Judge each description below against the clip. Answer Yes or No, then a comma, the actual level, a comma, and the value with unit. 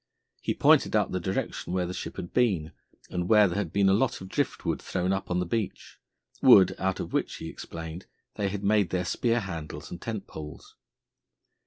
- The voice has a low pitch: Yes, very low, 95 Hz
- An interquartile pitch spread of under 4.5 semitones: Yes, narrow, 2.6 semitones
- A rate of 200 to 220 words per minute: Yes, fast, 205 wpm